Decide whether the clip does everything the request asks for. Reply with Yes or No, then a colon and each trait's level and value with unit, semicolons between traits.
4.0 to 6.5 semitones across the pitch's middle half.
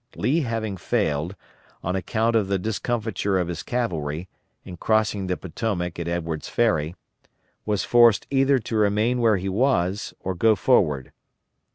Yes: average, 4.5 semitones